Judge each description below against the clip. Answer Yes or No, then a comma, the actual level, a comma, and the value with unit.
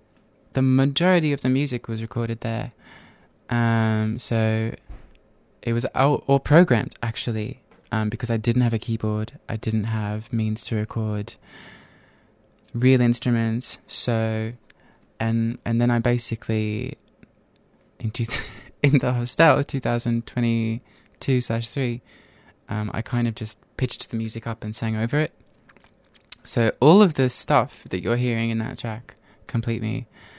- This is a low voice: Yes, low, 115 Hz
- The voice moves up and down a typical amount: No, narrow, 2.1 semitones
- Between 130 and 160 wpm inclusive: Yes, average, 140 wpm